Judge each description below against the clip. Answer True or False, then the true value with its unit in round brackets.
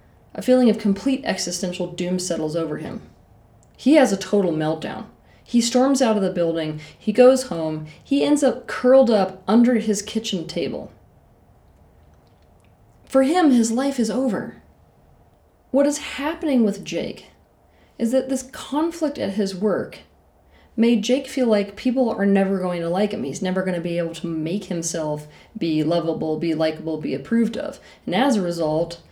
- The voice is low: False (200 Hz)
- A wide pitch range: True (7.1 semitones)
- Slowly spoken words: False (165 wpm)